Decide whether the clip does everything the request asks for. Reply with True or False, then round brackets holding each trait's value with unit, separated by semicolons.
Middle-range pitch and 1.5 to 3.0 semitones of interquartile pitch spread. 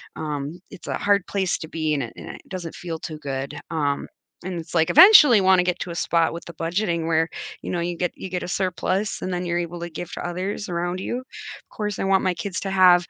True (175 Hz; 2.4 semitones)